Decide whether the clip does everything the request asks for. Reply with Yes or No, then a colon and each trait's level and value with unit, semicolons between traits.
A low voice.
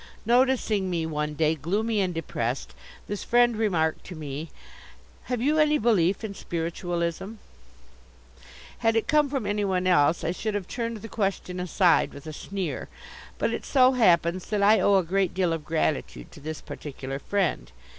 No: medium, 185 Hz